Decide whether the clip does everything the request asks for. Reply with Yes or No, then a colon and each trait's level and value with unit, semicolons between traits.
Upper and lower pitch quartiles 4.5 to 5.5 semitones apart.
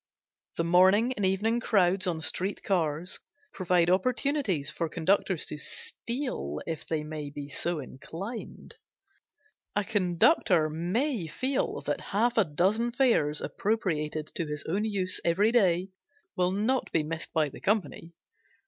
Yes: average, 5.2 semitones